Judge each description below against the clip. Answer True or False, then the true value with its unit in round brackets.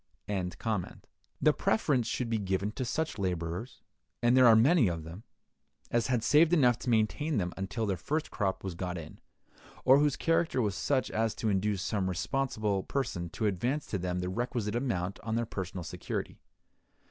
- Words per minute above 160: True (180 wpm)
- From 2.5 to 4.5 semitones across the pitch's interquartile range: False (5.1 semitones)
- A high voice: False (110 Hz)